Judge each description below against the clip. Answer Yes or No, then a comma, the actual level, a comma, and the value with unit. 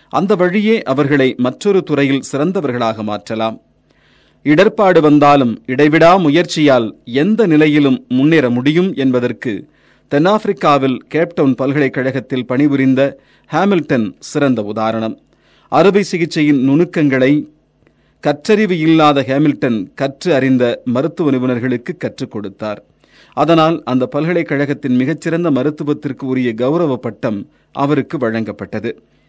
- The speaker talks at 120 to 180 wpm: No, average, 90 wpm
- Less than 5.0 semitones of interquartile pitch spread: Yes, average, 4.1 semitones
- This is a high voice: No, medium, 145 Hz